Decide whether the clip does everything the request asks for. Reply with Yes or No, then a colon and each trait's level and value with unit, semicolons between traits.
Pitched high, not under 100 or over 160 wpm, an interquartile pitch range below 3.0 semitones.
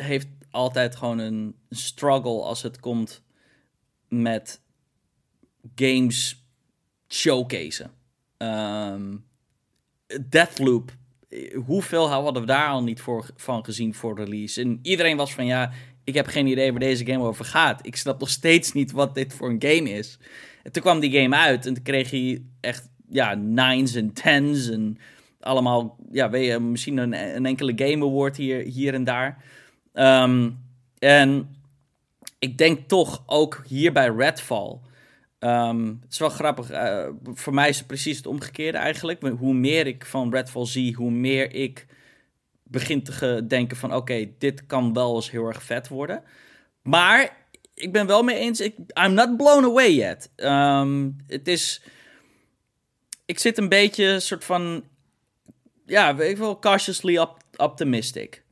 No: low, 130 Hz; average, 155 wpm; narrow, 2.6 semitones